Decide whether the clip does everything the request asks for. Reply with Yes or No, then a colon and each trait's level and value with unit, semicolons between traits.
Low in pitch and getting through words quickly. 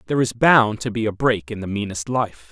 Yes: low, 110 Hz; fast, 265 wpm